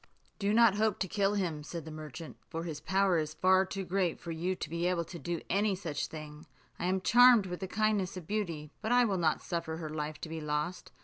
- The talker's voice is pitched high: No, medium, 175 Hz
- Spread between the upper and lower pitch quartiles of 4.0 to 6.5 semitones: No, average, 3.6 semitones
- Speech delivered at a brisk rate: Yes, fast, 240 wpm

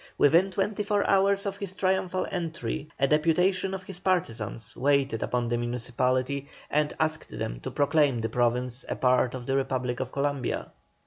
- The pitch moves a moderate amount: No, wide, 6.7 semitones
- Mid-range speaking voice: Yes, medium, 145 Hz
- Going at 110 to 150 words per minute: No, average, 170 wpm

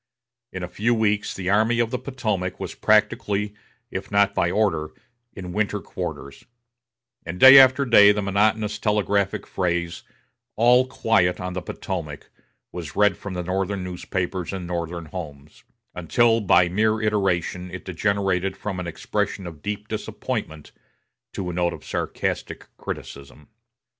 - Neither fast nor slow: Yes, average, 145 wpm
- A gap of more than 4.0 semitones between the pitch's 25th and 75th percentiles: No, average, 3.1 semitones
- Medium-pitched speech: No, very low, 95 Hz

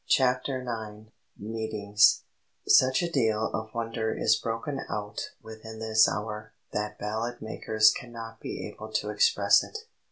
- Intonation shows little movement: Yes, narrow, 1.8 semitones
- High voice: No, low, 110 Hz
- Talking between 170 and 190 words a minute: No, slow, 135 wpm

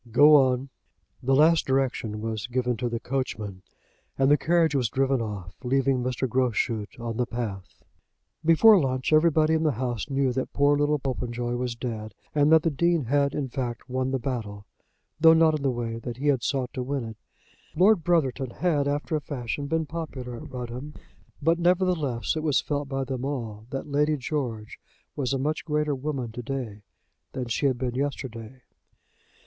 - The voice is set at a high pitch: No, low, 135 Hz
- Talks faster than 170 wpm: Yes, average, 185 wpm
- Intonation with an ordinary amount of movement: Yes, average, 3.5 semitones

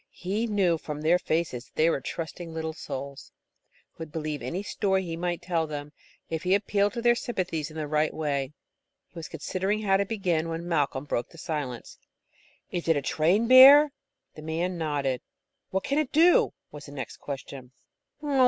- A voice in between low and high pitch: Yes, medium, 165 Hz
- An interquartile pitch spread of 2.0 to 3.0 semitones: No, average, 4.2 semitones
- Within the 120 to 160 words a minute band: No, average, 185 wpm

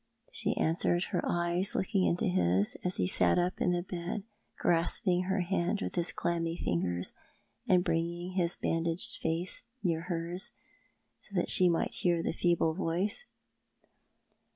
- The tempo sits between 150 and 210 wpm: Yes, average, 155 wpm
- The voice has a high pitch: No, medium, 175 Hz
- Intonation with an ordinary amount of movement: No, narrow, 1.7 semitones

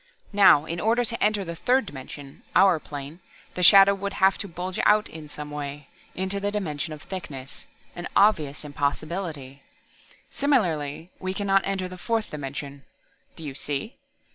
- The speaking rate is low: No, average, 165 wpm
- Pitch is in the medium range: Yes, medium, 175 Hz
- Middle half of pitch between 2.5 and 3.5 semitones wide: No, average, 5.3 semitones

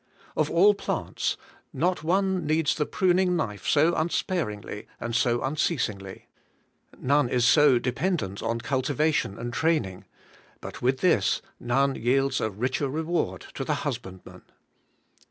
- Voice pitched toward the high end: No, medium, 140 Hz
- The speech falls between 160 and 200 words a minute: No, slow, 135 wpm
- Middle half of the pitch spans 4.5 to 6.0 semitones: Yes, wide, 5.5 semitones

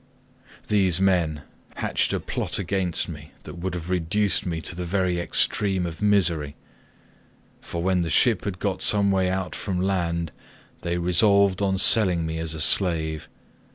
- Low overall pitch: Yes, very low, 90 Hz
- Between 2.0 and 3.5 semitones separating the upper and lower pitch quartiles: Yes, narrow, 2.5 semitones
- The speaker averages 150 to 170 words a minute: Yes, average, 160 wpm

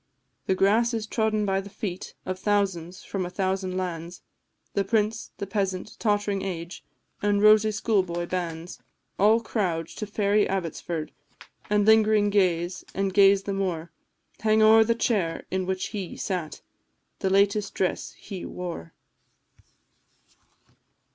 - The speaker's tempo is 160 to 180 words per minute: No, slow, 135 wpm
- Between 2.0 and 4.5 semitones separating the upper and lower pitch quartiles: Yes, narrow, 2.5 semitones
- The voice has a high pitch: Yes, high, 195 Hz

